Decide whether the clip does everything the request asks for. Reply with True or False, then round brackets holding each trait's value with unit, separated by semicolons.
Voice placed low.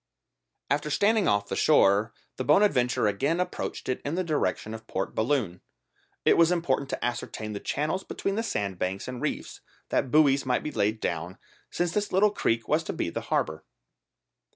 True (130 Hz)